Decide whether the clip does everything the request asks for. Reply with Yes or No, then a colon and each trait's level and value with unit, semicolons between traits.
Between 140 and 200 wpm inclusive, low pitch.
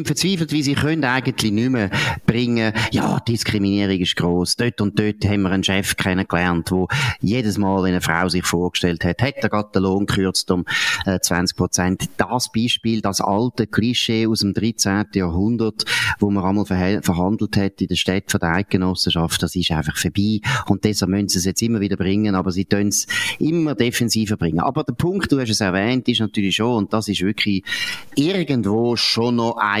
Yes: fast, 190 wpm; low, 100 Hz